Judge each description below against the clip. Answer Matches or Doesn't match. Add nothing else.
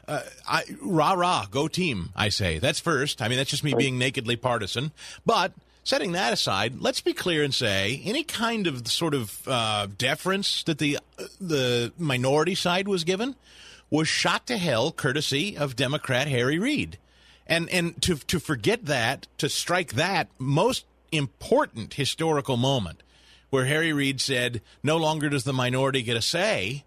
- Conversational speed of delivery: Matches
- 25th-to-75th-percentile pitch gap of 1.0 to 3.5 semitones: Doesn't match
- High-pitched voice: Doesn't match